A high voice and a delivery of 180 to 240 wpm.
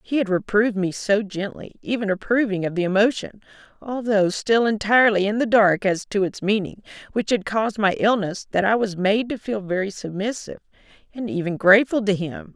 Yes: high, 205 Hz; average, 185 wpm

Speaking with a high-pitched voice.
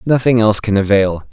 No: low, 110 Hz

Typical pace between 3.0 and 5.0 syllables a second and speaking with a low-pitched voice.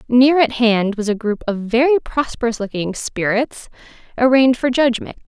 No: 4.9 syllables/s; high, 235 Hz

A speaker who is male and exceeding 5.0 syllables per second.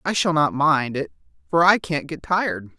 No: male; 4.8 syllables/s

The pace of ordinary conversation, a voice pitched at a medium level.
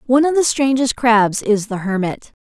No: average, 195 wpm; high, 235 Hz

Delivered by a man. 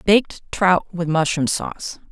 No: female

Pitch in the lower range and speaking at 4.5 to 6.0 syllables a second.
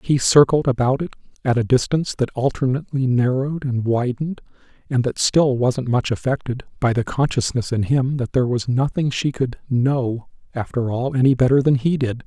Yes: low, 130 Hz; 5.3 syllables/s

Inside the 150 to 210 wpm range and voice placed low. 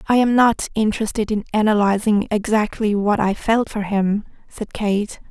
No: average, 160 wpm; high, 210 Hz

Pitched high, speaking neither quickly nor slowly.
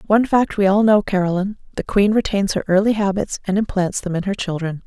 No: high, 195 Hz; fast, 220 wpm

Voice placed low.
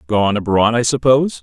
Yes: low, 115 Hz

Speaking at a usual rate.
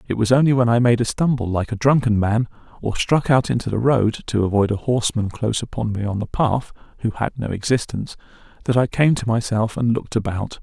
No: fast, 215 wpm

